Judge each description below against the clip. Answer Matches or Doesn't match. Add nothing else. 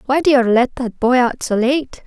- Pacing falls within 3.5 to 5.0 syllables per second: Matches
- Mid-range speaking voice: Doesn't match